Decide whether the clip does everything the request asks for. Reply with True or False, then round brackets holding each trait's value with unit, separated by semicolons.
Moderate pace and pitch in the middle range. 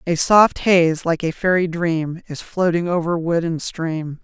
True (185 wpm; 170 Hz)